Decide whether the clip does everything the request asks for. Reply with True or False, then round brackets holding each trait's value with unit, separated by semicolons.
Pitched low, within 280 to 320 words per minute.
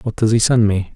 True (110 Hz; 315 wpm)